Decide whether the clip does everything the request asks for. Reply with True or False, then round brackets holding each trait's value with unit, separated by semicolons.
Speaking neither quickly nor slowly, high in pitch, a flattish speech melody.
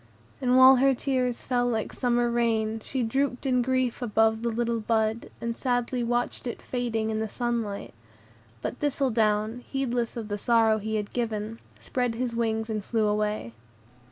True (165 wpm; 235 Hz; 2.0 semitones)